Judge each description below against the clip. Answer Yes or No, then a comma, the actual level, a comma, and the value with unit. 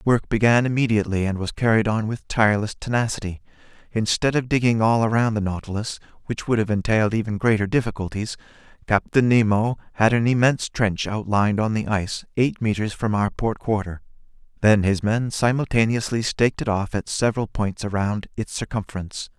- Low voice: Yes, low, 110 Hz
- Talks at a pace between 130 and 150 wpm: No, average, 165 wpm